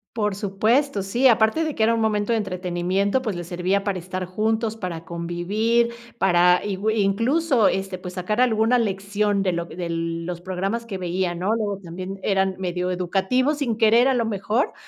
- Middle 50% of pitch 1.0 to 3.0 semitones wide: No, average, 3.6 semitones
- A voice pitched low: No, high, 195 Hz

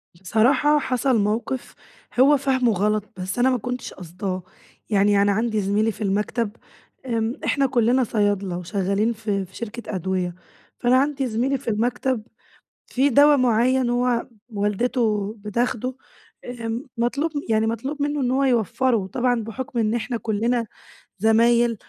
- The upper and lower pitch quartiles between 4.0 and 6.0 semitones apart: No, average, 3.4 semitones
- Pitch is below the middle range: No, high, 230 Hz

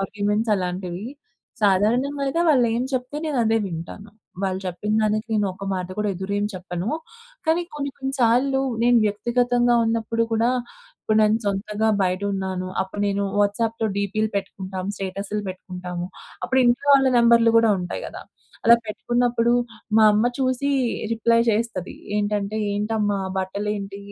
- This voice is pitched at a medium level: No, high, 210 Hz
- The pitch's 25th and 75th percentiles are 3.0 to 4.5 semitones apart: Yes, average, 3.3 semitones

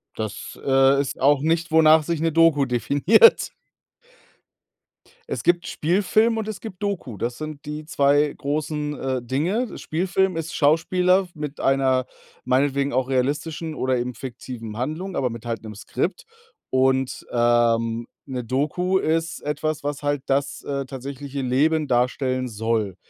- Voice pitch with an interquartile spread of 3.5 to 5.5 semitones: Yes, average, 3.9 semitones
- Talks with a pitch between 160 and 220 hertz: No, medium, 140 Hz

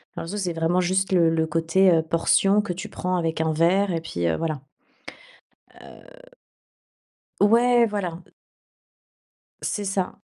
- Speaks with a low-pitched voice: No, medium, 180 Hz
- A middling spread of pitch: Yes, average, 3.5 semitones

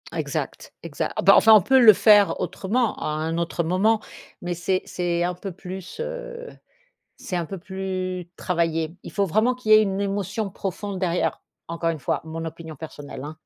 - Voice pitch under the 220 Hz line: Yes, medium, 185 Hz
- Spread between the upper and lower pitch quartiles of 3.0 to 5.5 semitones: Yes, average, 3.6 semitones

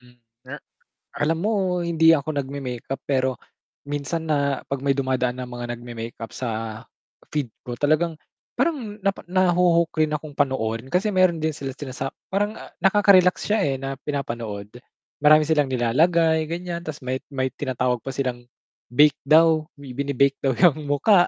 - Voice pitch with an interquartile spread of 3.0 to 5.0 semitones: Yes, average, 4.5 semitones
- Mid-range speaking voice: Yes, medium, 145 Hz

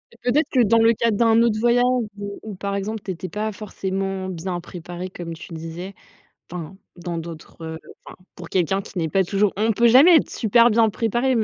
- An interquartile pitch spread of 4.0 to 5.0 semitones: Yes, average, 4.3 semitones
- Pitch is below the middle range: No, high, 200 Hz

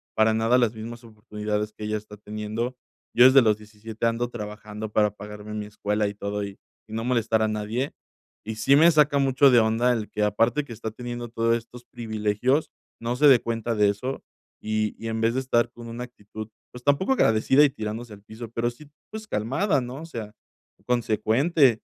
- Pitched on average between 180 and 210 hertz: No, low, 115 Hz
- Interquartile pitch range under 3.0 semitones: Yes, narrow, 2.5 semitones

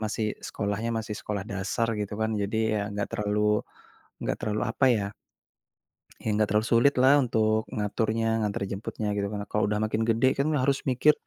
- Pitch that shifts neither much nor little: No, narrow, 1.6 semitones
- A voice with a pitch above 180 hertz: No, low, 110 Hz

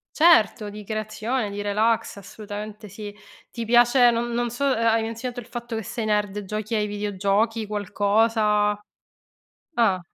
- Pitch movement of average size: No, narrow, 2.0 semitones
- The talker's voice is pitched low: No, high, 215 Hz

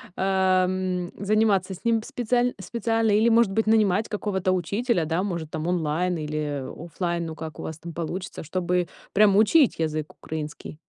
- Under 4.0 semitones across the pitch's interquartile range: No, average, 4.6 semitones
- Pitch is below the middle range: No, medium, 185 Hz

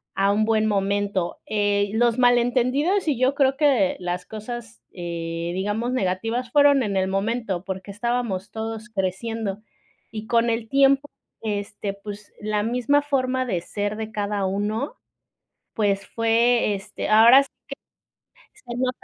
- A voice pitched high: Yes, high, 220 Hz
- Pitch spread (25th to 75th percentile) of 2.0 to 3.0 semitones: No, average, 3.5 semitones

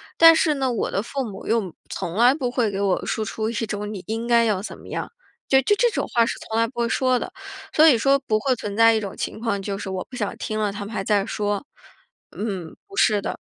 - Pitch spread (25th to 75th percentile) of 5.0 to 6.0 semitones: No, average, 3.4 semitones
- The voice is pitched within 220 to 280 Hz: Yes, high, 225 Hz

